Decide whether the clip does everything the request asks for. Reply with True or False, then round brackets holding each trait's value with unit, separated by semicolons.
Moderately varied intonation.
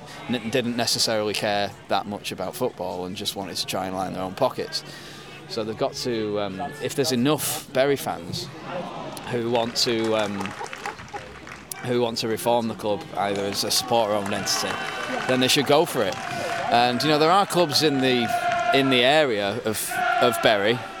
True (4.5 semitones)